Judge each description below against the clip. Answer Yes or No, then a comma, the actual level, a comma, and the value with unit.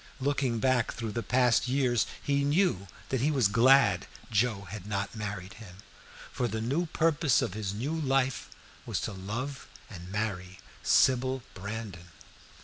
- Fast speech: No, average, 150 wpm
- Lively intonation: No, average, 4.8 semitones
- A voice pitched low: Yes, low, 115 Hz